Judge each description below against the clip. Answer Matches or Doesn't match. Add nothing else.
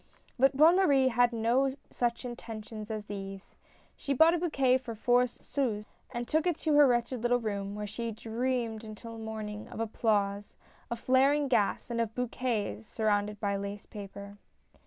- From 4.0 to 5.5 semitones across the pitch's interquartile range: Doesn't match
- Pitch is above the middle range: Matches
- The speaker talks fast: Doesn't match